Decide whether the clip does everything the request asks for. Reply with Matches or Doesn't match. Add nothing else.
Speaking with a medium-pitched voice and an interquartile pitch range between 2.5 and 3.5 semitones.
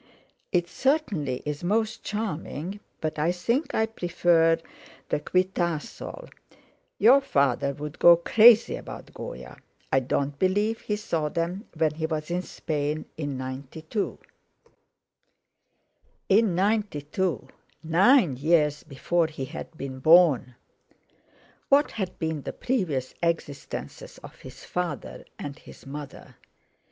Doesn't match